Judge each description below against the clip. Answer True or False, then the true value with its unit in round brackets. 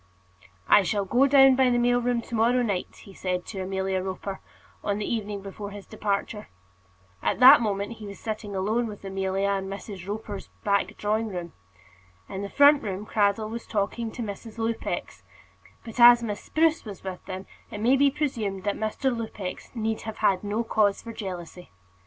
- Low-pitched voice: False (210 Hz)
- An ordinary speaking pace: True (185 wpm)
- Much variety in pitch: False (3.0 semitones)